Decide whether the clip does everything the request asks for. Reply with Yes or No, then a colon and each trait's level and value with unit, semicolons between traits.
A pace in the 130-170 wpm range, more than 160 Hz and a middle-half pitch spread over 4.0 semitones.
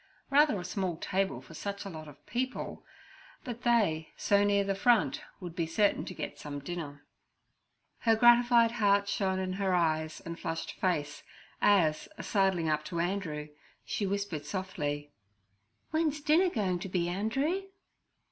Yes: average, 155 wpm; high, 190 Hz; average, 5.2 semitones